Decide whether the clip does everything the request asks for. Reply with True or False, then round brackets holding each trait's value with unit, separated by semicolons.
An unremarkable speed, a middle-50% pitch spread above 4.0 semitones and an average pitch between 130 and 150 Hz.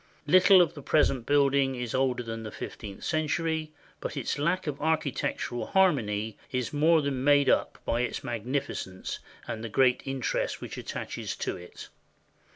True (165 wpm; 4.4 semitones; 135 Hz)